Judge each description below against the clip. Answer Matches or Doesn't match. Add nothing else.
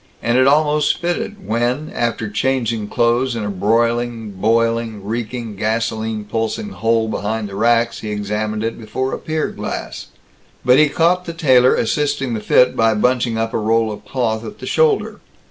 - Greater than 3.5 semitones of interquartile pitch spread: Doesn't match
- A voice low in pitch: Matches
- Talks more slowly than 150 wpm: Doesn't match